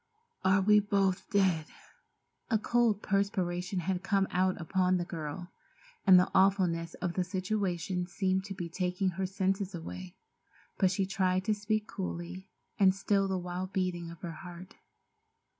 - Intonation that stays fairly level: Yes, narrow, 1.7 semitones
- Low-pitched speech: No, medium, 185 Hz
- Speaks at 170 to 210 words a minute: No, average, 155 wpm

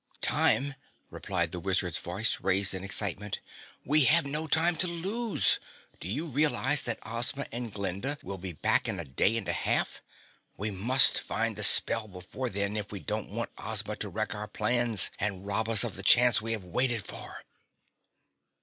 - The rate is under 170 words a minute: No, average, 180 wpm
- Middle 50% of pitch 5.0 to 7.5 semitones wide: Yes, average, 5.3 semitones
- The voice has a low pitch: Yes, low, 110 Hz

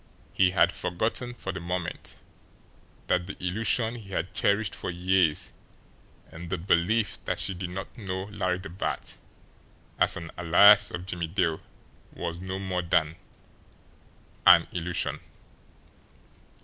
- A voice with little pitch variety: Yes, narrow, 2.1 semitones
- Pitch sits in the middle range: No, very low, 90 Hz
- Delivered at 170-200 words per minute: No, slow, 135 wpm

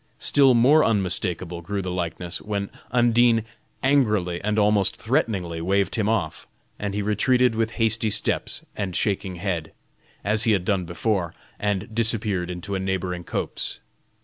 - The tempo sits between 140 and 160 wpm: Yes, average, 150 wpm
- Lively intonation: No, average, 3.7 semitones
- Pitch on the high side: No, low, 100 Hz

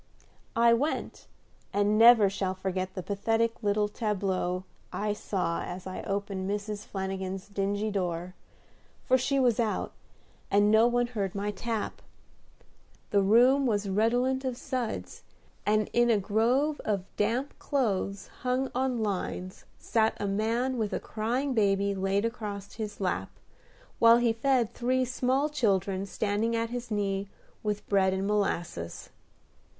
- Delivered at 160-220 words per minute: No, average, 140 wpm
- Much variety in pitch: No, average, 3.4 semitones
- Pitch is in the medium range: No, high, 210 Hz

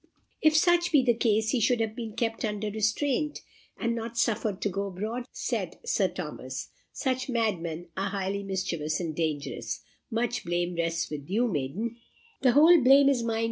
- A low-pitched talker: No, high, 220 Hz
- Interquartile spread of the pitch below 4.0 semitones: No, average, 4.6 semitones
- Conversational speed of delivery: Yes, average, 175 wpm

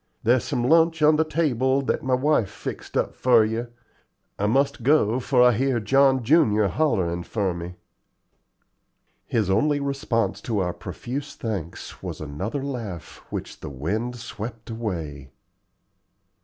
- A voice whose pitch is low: Yes, low, 120 Hz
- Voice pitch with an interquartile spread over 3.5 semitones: Yes, average, 5.2 semitones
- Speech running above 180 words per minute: No, average, 140 wpm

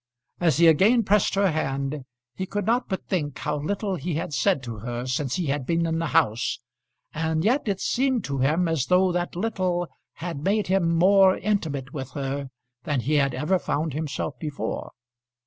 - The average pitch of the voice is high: No, medium, 165 Hz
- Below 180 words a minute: No, average, 190 wpm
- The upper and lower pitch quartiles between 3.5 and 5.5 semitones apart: Yes, average, 5.1 semitones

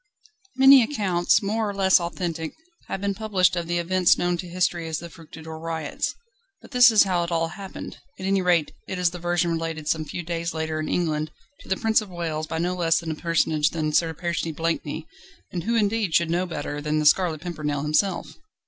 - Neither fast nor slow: No, fast, 210 wpm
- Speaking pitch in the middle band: Yes, medium, 170 Hz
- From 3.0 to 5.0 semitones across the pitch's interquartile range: No, narrow, 2.6 semitones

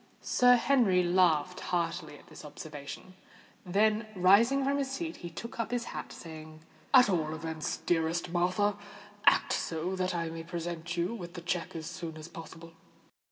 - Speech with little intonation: No, average, 3.9 semitones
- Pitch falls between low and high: Yes, medium, 175 Hz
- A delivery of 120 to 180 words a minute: Yes, average, 165 wpm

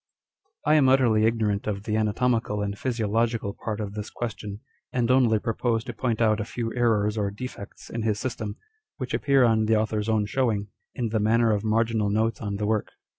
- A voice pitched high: No, low, 110 Hz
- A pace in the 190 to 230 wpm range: Yes, average, 200 wpm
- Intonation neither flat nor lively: No, narrow, 1.9 semitones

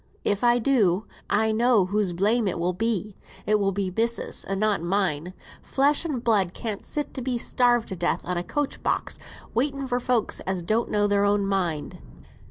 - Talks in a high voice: Yes, high, 210 Hz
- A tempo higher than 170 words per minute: Yes, average, 190 wpm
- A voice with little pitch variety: No, average, 4.1 semitones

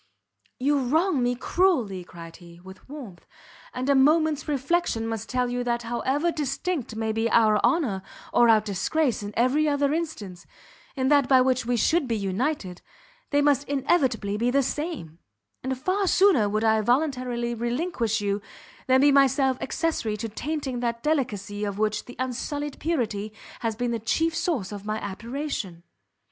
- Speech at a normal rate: Yes, average, 165 wpm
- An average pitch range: Yes, average, 5.0 semitones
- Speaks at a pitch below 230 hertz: No, high, 245 Hz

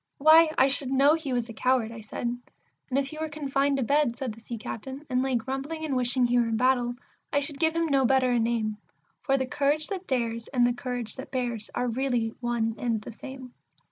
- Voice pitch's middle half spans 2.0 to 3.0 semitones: Yes, average, 2.7 semitones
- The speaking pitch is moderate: No, very high, 255 Hz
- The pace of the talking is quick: Yes, fast, 235 wpm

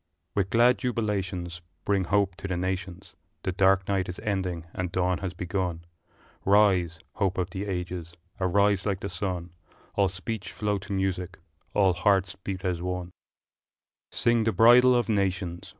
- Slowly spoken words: No, average, 160 wpm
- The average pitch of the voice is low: Yes, very low, 95 Hz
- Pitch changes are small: Yes, narrow, 2.1 semitones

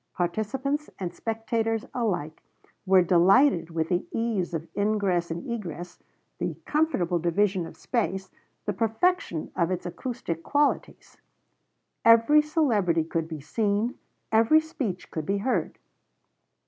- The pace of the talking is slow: Yes, slow, 120 wpm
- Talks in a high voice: Yes, high, 200 Hz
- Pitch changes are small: No, average, 5.3 semitones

